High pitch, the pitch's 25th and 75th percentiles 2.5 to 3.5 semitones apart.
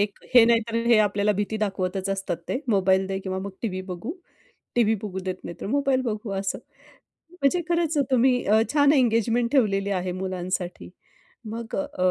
No: high, 210 Hz; average, 4.2 semitones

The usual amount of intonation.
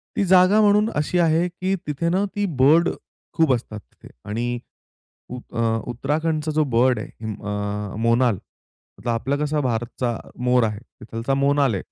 No: wide, 5.9 semitones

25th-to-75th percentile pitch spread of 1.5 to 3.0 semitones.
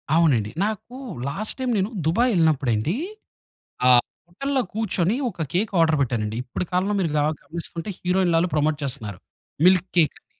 No: average, 5.0 semitones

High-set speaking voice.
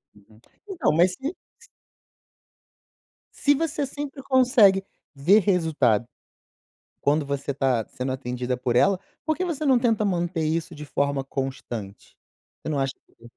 No: medium, 160 Hz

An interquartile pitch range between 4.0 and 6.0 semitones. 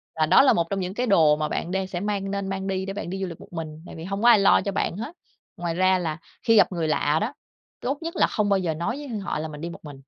No: average, 3.5 semitones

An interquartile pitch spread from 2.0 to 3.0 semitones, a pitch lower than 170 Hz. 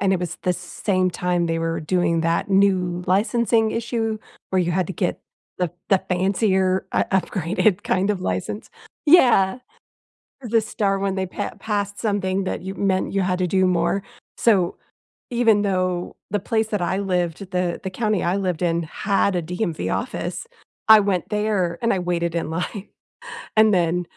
No: narrow, 2.4 semitones; high, 190 Hz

